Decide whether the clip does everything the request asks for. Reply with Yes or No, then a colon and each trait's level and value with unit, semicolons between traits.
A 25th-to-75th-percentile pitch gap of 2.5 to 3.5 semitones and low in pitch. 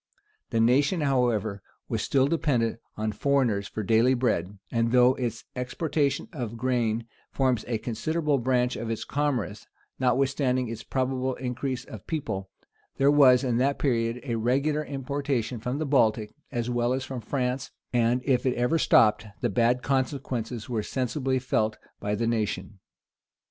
Yes: average, 2.8 semitones; low, 125 Hz